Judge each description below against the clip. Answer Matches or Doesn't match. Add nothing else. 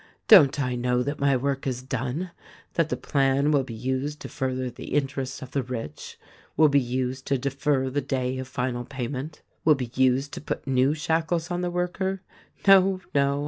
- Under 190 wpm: Doesn't match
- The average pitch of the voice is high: Doesn't match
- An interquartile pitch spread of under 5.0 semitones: Matches